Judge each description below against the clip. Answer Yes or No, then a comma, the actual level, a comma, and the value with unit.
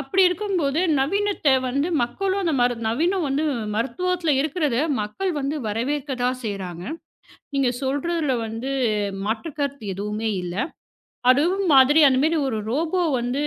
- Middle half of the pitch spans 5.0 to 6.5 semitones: Yes, wide, 5.5 semitones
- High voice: Yes, very high, 275 Hz